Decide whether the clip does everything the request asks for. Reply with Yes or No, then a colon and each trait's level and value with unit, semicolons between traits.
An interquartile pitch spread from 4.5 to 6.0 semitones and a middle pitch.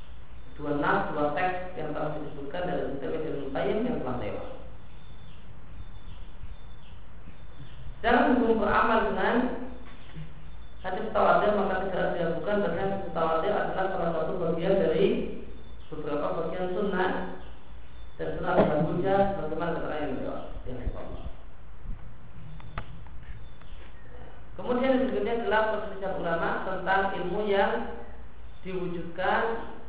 Yes: average, 5.3 semitones; medium, 180 Hz